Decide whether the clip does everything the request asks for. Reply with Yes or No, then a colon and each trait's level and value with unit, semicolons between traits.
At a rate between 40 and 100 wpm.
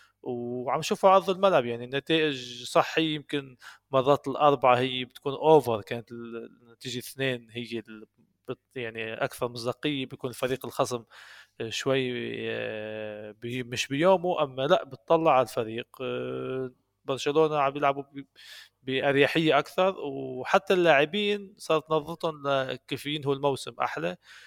No: average, 115 wpm